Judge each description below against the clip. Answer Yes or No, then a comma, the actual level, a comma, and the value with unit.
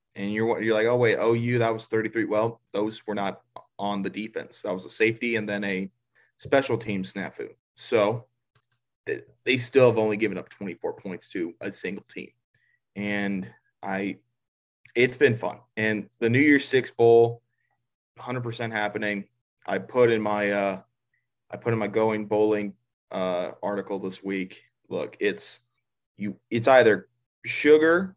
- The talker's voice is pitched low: Yes, low, 110 Hz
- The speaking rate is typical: Yes, average, 160 wpm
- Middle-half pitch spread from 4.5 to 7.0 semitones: No, average, 2.9 semitones